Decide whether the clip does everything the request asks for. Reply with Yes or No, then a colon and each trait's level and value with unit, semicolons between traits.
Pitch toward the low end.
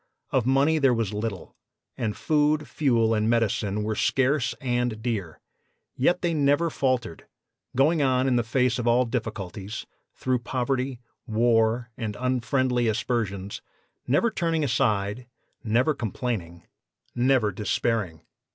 Yes: low, 120 Hz